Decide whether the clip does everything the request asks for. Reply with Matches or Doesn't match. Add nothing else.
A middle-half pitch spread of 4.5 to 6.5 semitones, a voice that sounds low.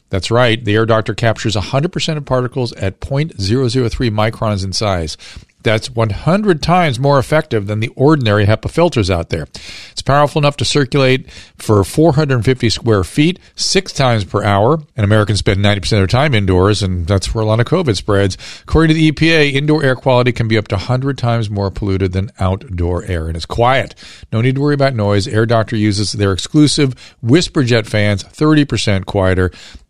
Matches